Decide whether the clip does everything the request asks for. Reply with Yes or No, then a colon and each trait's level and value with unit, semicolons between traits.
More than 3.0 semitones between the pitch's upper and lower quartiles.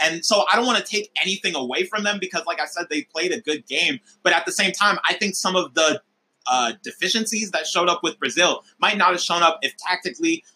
Yes: average, 3.9 semitones